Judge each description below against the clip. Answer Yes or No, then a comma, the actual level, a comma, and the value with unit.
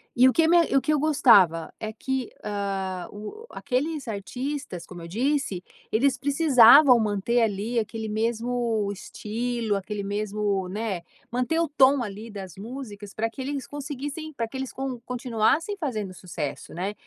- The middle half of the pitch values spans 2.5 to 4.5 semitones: No, average, 4.9 semitones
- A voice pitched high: Yes, high, 230 Hz